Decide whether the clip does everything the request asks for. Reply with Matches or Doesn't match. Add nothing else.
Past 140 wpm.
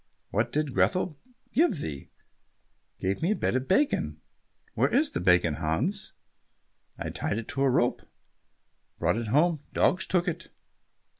Matches